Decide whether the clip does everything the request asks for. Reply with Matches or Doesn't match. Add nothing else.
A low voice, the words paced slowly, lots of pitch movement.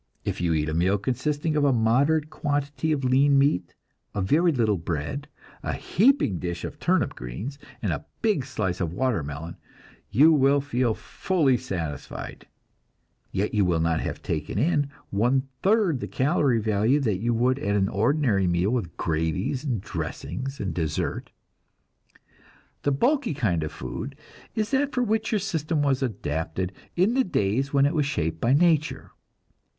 Doesn't match